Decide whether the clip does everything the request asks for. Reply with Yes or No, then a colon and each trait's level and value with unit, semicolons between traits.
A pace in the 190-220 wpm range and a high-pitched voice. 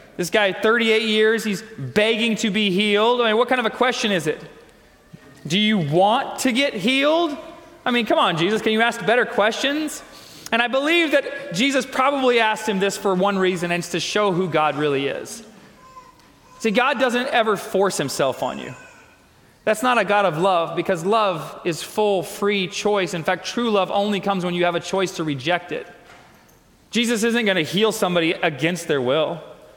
Yes: average, 195 wpm; high, 210 Hz